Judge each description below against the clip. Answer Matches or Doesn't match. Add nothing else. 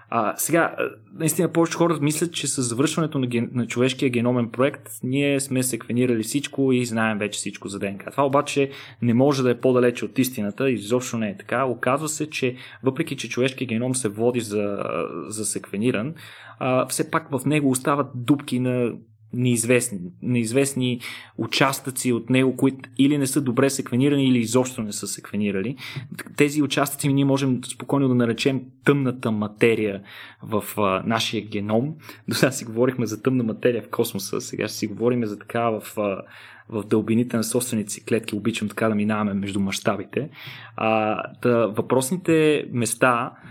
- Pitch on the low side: Matches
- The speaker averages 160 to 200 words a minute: Matches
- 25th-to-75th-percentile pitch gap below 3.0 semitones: Doesn't match